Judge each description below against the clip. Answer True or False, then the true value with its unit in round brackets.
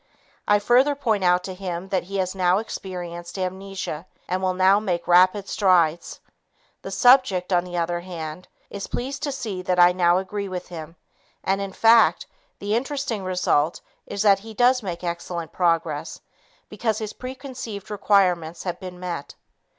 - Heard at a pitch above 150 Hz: True (185 Hz)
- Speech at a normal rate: True (165 wpm)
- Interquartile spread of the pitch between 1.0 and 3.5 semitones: True (2.8 semitones)